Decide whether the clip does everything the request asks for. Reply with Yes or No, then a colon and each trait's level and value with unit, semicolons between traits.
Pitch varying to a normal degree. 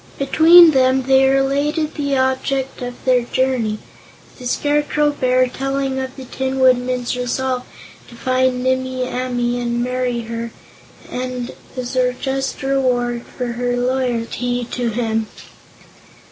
No: narrow, 1.4 semitones